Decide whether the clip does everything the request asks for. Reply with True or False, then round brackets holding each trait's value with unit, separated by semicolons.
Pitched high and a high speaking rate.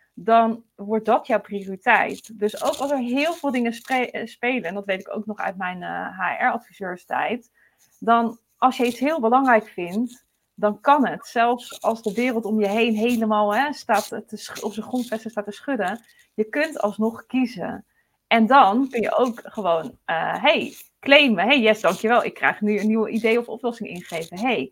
False (225 Hz; 190 wpm)